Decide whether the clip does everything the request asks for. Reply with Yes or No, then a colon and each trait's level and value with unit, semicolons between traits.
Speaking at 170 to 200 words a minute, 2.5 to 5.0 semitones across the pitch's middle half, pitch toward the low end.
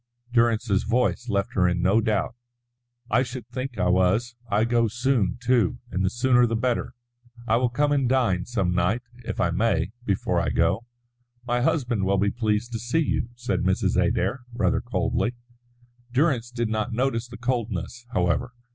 Yes: average, 175 wpm; average, 3.9 semitones; low, 115 Hz